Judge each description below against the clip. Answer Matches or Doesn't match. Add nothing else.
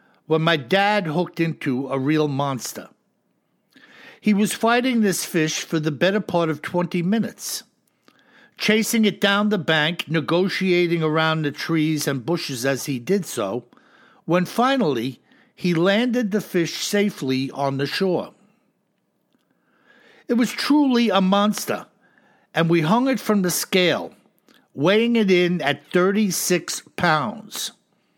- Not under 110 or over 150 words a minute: Matches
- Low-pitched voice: Doesn't match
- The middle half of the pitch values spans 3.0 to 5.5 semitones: Matches